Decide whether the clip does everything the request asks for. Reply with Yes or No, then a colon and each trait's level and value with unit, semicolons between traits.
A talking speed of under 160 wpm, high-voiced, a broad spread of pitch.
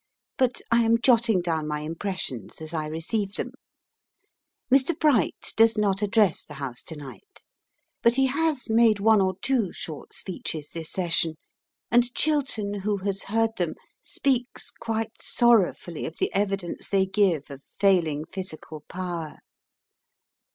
Yes: average, 145 wpm; high, 195 Hz; wide, 5.9 semitones